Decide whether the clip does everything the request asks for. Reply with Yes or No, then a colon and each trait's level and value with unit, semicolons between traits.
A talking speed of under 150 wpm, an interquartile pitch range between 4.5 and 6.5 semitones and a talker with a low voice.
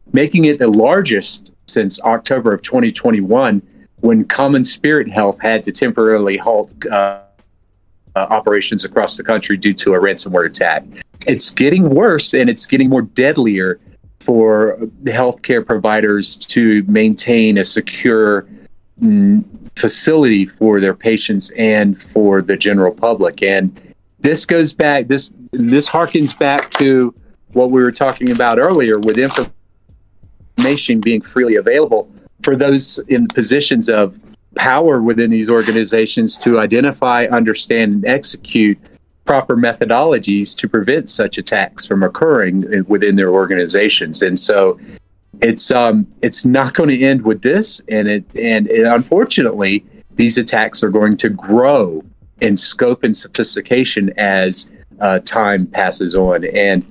Yes: average, 140 wpm; average, 5.1 semitones; low, 110 Hz